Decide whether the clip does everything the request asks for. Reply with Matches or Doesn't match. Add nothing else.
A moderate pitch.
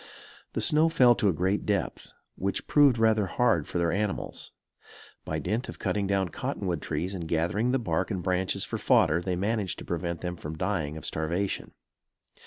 Doesn't match